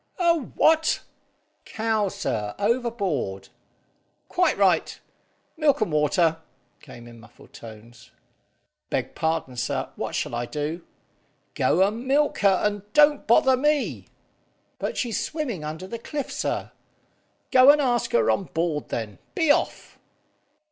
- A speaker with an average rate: No, slow, 130 wpm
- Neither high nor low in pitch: No, high, 205 Hz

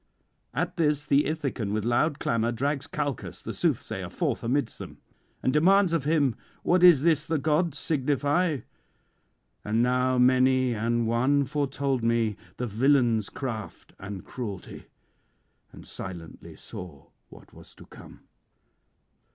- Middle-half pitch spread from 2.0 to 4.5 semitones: Yes, average, 4.2 semitones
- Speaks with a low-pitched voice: Yes, low, 130 Hz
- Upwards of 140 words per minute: No, slow, 135 wpm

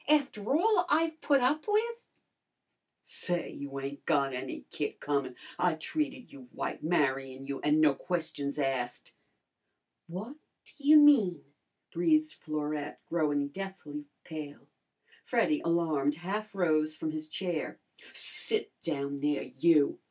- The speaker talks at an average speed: No, slow, 130 wpm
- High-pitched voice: No, medium, 160 Hz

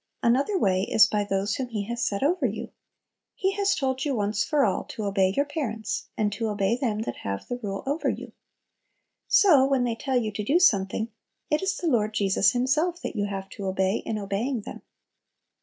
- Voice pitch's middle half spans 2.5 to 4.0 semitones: No, average, 5.3 semitones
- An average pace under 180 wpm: No, fast, 205 wpm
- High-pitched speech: Yes, high, 225 Hz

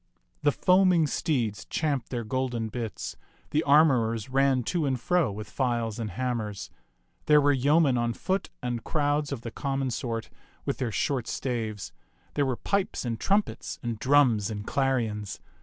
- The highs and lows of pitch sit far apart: No, average, 4.1 semitones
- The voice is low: Yes, low, 130 Hz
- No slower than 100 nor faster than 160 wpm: Yes, average, 155 wpm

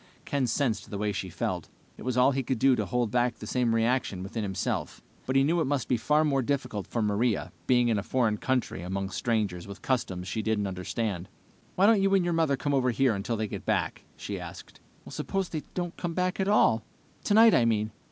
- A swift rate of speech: Yes, fast, 225 wpm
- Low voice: Yes, low, 120 Hz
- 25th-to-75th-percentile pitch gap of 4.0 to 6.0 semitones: Yes, average, 5.0 semitones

